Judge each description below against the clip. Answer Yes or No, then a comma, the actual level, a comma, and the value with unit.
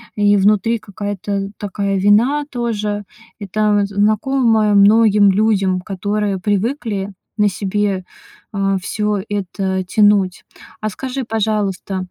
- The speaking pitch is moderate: No, high, 205 Hz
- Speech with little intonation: Yes, narrow, 1.6 semitones